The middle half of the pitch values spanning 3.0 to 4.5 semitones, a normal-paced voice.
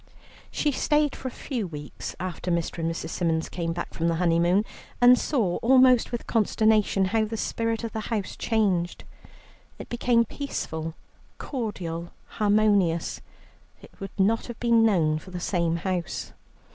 No: average, 5.2 semitones; average, 155 wpm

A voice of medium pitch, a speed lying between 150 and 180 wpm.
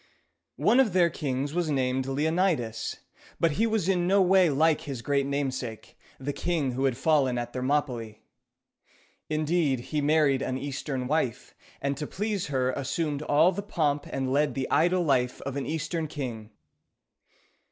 Yes: medium, 145 Hz; average, 160 wpm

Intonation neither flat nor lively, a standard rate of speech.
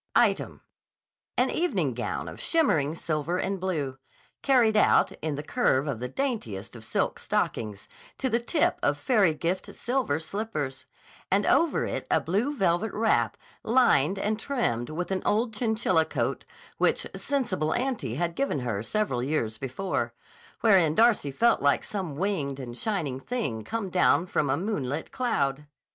No: wide, 8.2 semitones; average, 155 wpm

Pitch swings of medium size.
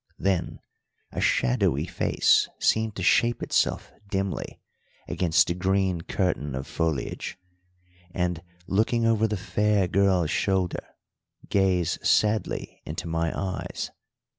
Yes: average, 3.0 semitones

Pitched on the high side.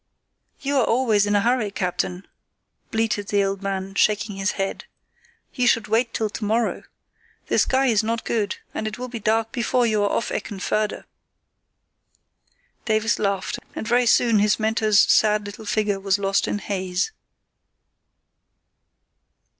Yes: high, 215 Hz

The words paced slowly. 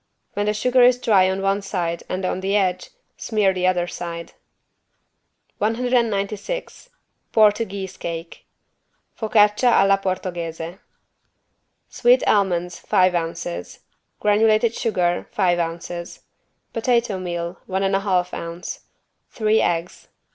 Yes: slow, 115 wpm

